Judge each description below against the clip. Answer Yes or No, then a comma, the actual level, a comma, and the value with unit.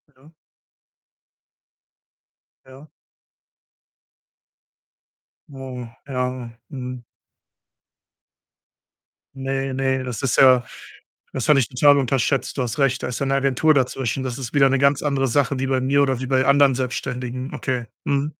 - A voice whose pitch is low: Yes, low, 130 Hz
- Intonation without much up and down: Yes, narrow, 1.4 semitones